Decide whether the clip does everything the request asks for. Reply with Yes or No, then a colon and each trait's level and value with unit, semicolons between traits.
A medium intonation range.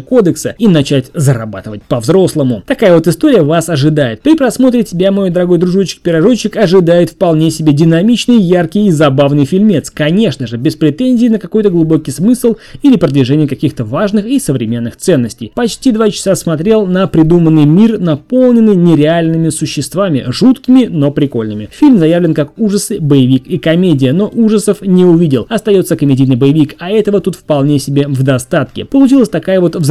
No: wide, 6.2 semitones